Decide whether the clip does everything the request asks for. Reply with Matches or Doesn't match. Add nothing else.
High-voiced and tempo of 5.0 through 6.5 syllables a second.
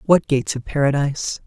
Doesn't match